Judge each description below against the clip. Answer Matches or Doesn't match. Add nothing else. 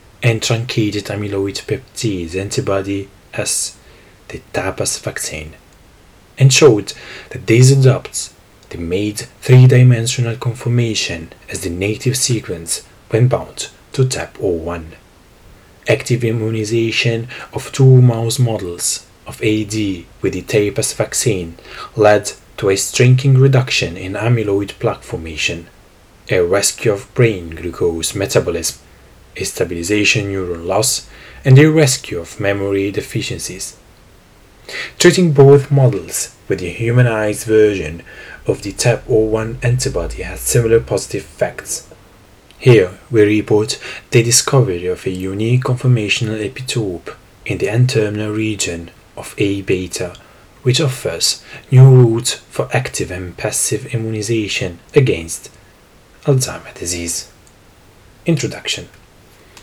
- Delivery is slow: Matches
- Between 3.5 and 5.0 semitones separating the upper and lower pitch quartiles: Matches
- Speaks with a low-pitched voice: Matches